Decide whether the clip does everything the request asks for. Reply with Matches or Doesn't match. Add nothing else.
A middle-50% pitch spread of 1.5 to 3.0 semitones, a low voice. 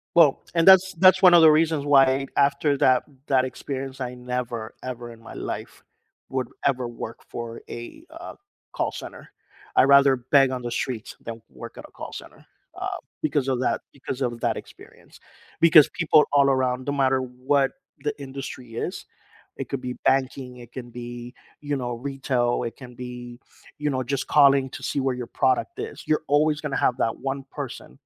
Matches